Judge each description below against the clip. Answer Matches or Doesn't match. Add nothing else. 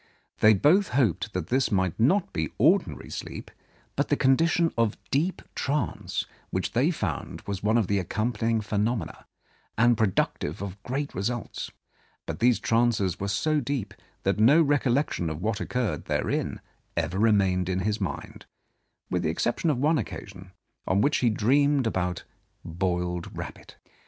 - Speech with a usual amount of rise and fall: Doesn't match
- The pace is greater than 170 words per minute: Doesn't match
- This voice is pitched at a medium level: Doesn't match